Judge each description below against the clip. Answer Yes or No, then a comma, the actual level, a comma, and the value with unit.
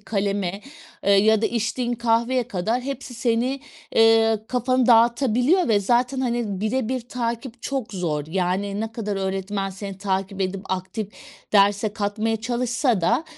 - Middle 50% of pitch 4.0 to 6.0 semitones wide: No, average, 3.5 semitones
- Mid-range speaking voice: No, high, 225 Hz